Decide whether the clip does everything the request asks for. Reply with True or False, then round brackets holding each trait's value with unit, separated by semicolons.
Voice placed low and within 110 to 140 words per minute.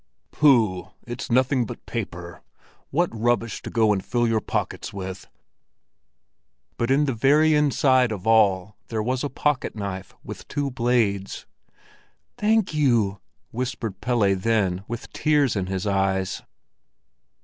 True (115 Hz; 135 wpm)